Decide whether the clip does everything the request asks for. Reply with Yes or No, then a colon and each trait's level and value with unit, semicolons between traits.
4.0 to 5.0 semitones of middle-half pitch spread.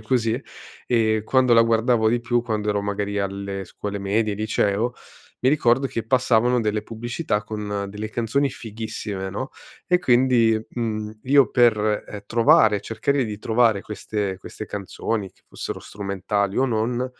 No: average, 2.7 semitones